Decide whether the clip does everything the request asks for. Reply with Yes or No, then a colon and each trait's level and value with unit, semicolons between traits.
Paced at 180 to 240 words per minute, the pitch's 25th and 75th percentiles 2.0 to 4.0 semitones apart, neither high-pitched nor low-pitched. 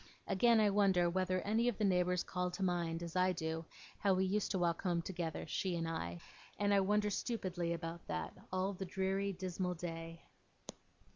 Yes: average, 190 wpm; narrow, 2.4 semitones; medium, 180 Hz